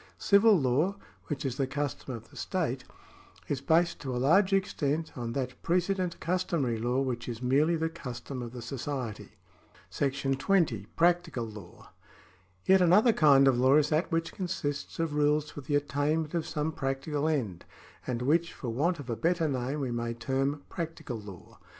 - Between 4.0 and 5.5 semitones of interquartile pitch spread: Yes, average, 4.6 semitones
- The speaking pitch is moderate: Yes, medium, 145 Hz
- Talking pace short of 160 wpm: No, average, 175 wpm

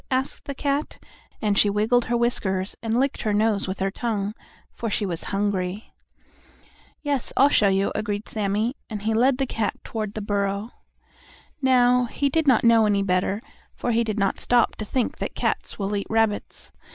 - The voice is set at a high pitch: Yes, high, 215 Hz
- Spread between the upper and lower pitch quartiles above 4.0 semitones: No, average, 3.3 semitones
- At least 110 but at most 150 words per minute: No, average, 185 wpm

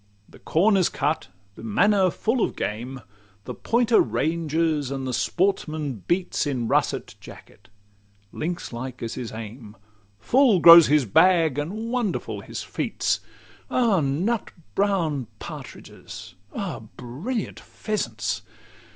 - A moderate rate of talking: No, slow, 125 wpm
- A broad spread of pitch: Yes, wide, 7.6 semitones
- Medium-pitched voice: Yes, medium, 155 Hz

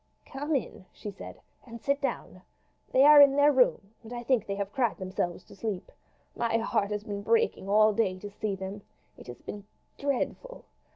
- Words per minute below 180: No, average, 190 wpm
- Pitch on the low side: No, high, 215 Hz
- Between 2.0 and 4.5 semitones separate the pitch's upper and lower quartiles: No, average, 5.3 semitones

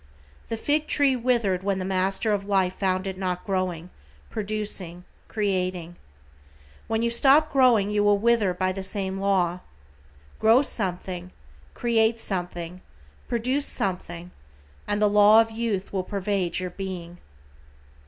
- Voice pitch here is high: Yes, high, 195 Hz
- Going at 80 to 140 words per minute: Yes, slow, 135 wpm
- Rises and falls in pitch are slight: No, average, 3.3 semitones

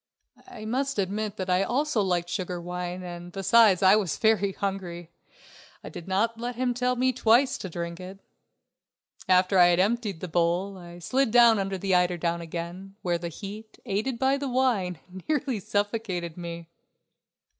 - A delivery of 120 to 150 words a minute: No, average, 165 wpm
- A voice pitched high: Yes, high, 195 Hz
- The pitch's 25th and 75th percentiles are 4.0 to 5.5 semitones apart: Yes, average, 4.4 semitones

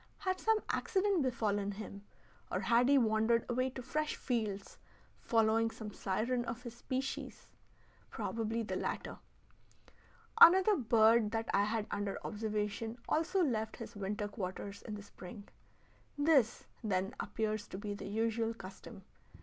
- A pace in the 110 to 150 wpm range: Yes, average, 140 wpm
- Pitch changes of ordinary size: Yes, average, 3.1 semitones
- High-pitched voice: Yes, high, 225 Hz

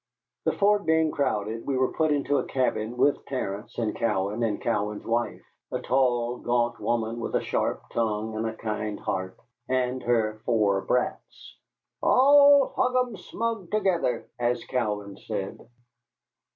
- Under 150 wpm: Yes, average, 140 wpm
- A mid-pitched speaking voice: No, low, 120 Hz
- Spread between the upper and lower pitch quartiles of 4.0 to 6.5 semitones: Yes, average, 4.9 semitones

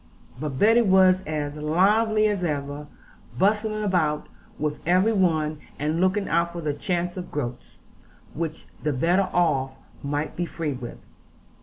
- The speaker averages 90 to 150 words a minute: Yes, average, 145 wpm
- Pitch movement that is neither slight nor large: Yes, average, 4.2 semitones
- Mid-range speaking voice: Yes, medium, 170 Hz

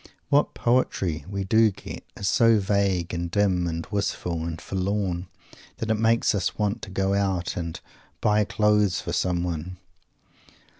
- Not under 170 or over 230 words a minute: No, average, 150 wpm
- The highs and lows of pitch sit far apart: No, average, 3.2 semitones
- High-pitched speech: No, very low, 95 Hz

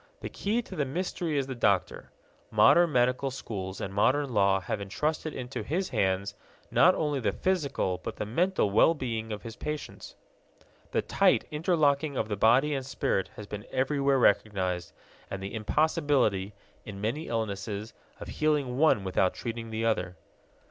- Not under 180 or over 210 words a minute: No, average, 160 wpm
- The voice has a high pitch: No, low, 120 Hz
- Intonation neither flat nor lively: No, wide, 6.6 semitones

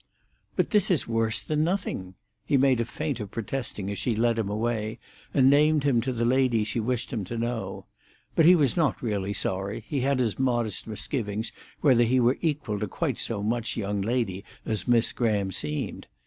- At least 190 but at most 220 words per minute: Yes, average, 195 wpm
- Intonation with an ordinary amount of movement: Yes, average, 3.9 semitones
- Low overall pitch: Yes, low, 115 Hz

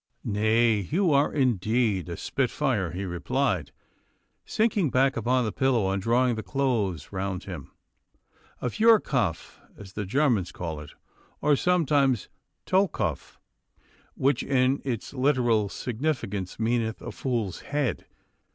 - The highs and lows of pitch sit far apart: Yes, wide, 5.7 semitones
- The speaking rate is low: Yes, slow, 125 wpm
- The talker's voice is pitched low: Yes, low, 120 Hz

